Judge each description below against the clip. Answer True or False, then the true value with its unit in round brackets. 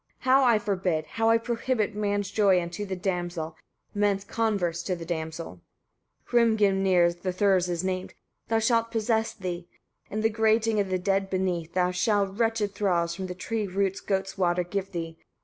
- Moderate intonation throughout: True (3.4 semitones)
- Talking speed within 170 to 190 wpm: True (175 wpm)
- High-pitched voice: True (195 Hz)